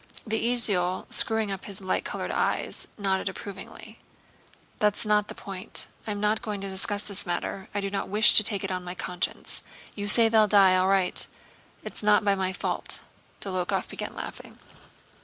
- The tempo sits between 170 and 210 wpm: Yes, average, 175 wpm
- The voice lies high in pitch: Yes, high, 200 Hz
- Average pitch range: No, narrow, 1.8 semitones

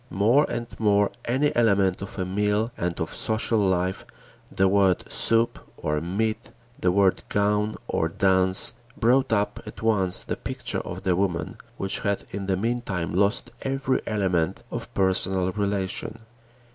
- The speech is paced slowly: No, average, 150 wpm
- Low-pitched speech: Yes, low, 100 Hz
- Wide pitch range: No, average, 2.9 semitones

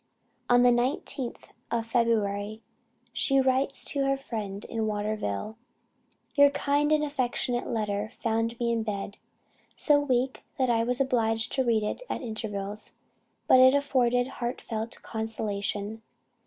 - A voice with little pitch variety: No, average, 3.2 semitones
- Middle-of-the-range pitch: No, high, 235 Hz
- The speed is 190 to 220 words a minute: No, slow, 135 wpm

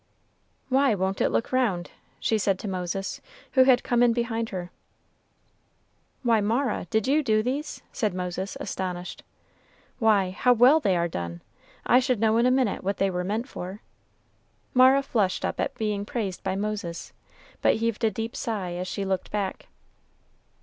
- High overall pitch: Yes, high, 215 Hz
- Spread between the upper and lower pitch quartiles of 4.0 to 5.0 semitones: Yes, average, 4.3 semitones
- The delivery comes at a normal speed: Yes, average, 170 wpm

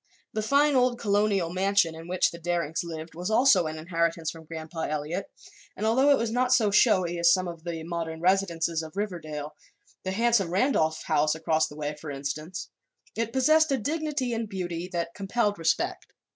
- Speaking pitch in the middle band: Yes, medium, 175 Hz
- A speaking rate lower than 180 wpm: No, average, 185 wpm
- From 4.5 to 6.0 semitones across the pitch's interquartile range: Yes, average, 5.2 semitones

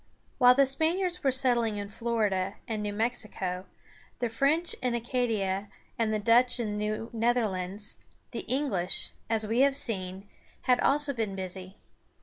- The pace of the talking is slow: No, average, 150 wpm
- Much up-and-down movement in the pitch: No, average, 3.7 semitones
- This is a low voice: No, high, 225 Hz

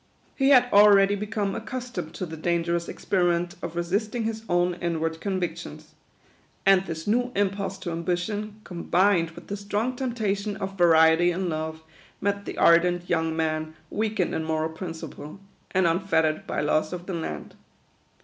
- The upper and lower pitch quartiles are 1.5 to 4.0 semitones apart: Yes, average, 3.6 semitones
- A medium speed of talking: Yes, average, 160 wpm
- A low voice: No, medium, 180 Hz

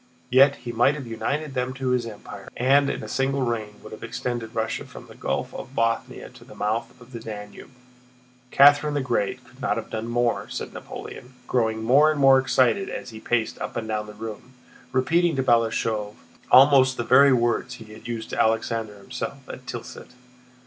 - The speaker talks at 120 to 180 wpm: No, average, 195 wpm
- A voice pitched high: No, low, 120 Hz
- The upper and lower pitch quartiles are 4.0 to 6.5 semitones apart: No, average, 2.9 semitones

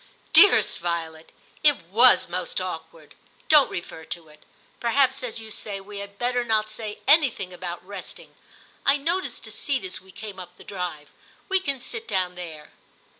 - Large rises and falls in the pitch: Yes, wide, 6.3 semitones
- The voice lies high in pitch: Yes, high, 200 Hz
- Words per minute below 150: No, average, 175 wpm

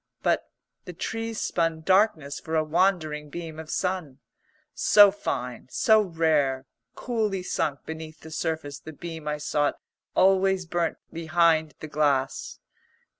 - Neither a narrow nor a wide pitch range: Yes, average, 3.6 semitones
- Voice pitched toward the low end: No, medium, 160 Hz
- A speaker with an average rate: No, slow, 130 wpm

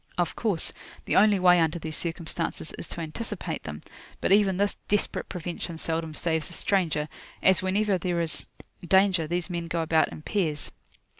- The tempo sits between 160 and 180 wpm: Yes, average, 170 wpm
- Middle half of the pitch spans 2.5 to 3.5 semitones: Yes, average, 2.8 semitones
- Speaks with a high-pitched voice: No, medium, 175 Hz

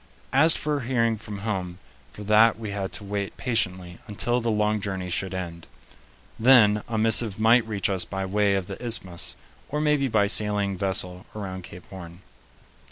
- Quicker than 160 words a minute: Yes, average, 170 wpm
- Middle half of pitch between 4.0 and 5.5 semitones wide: No, average, 3.2 semitones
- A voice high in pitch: No, low, 105 Hz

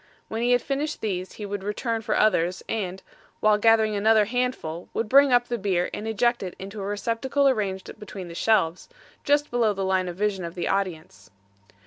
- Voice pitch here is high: Yes, high, 210 Hz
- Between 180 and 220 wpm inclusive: Yes, average, 195 wpm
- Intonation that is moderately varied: Yes, average, 3.6 semitones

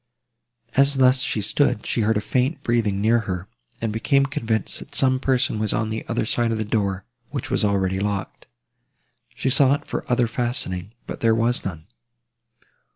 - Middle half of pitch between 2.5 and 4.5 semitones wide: Yes, average, 3.6 semitones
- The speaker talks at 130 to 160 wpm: No, average, 175 wpm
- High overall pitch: No, low, 115 Hz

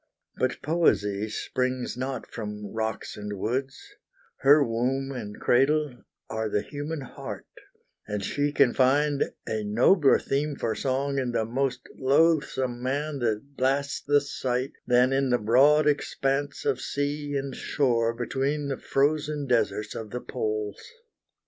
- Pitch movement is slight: No, average, 3.5 semitones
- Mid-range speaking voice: No, low, 130 Hz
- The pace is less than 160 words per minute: Yes, average, 140 wpm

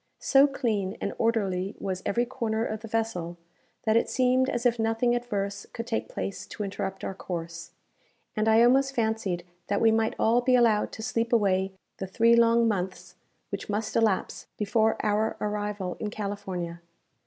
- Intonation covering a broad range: No, average, 3.0 semitones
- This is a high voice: Yes, high, 220 Hz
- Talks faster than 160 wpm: Yes, average, 170 wpm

